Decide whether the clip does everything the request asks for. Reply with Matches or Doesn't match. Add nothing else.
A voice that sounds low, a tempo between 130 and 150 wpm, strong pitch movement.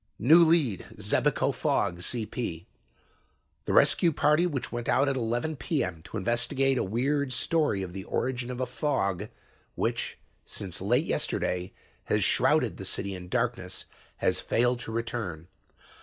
Matches